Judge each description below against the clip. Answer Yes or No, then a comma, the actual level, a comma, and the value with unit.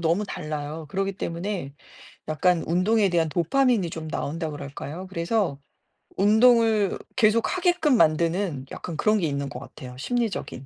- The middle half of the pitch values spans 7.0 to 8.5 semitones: No, wide, 5.5 semitones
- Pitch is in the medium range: Yes, medium, 175 Hz